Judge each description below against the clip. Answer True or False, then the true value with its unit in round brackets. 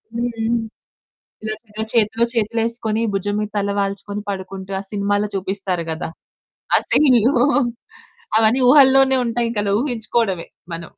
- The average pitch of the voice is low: False (215 Hz)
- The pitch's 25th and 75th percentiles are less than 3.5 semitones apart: True (2.8 semitones)